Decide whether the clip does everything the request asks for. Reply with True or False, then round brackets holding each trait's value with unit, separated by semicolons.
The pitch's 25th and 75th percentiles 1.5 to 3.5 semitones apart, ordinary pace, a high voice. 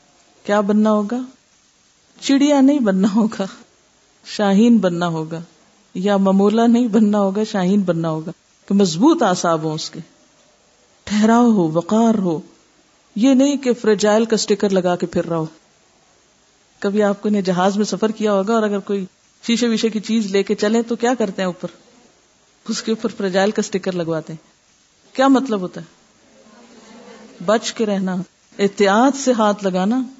True (3.2 semitones; 160 wpm; 210 Hz)